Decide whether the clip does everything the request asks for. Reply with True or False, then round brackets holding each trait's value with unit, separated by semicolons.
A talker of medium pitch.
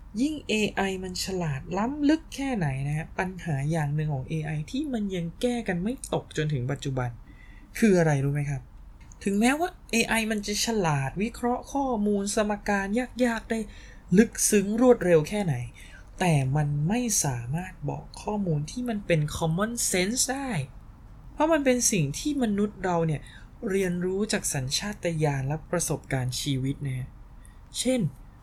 True (180 Hz)